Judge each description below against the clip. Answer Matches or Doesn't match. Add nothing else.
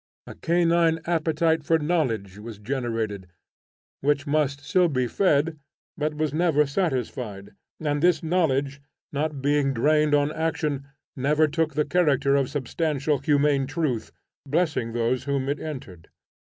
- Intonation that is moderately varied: Matches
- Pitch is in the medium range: Matches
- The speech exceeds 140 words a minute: Doesn't match